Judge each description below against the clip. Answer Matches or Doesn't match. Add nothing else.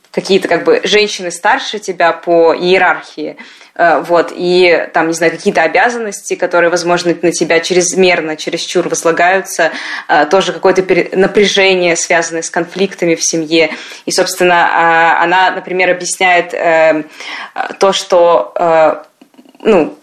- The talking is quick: Doesn't match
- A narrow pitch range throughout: Matches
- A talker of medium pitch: Matches